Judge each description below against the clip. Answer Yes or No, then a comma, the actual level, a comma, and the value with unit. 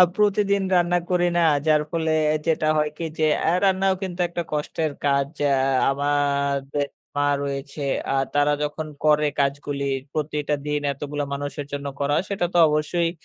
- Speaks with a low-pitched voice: No, medium, 150 Hz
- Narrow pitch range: No, average, 3.2 semitones